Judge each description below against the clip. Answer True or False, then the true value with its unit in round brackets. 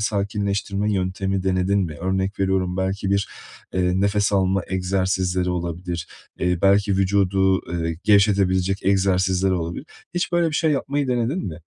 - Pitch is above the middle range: False (95 Hz)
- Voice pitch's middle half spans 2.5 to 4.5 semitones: False (1.6 semitones)